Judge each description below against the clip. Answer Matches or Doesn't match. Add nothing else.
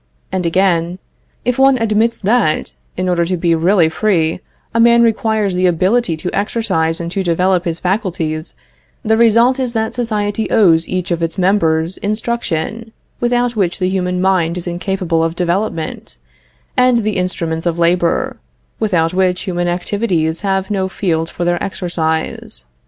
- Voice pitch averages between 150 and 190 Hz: Matches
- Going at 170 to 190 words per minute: Doesn't match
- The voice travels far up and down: Doesn't match